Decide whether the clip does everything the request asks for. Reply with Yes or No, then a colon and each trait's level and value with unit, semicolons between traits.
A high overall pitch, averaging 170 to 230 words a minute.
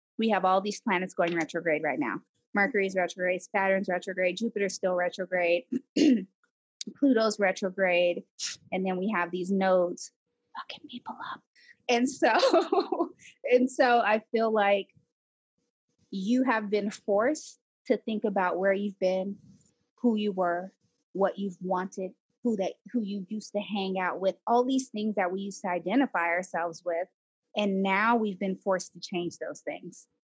No: high, 195 Hz; average, 155 wpm